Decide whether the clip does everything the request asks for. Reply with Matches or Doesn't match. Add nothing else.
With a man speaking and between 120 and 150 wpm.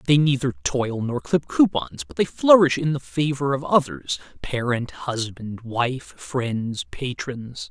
Matches